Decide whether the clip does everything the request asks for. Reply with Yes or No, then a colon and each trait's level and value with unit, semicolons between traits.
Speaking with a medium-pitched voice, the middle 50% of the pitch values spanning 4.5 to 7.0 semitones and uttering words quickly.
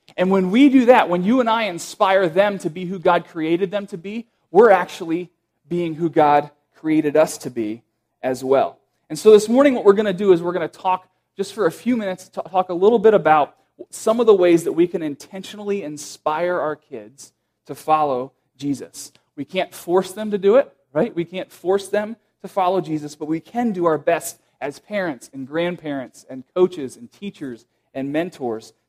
Yes: medium, 175 Hz; average, 5.0 semitones; fast, 210 wpm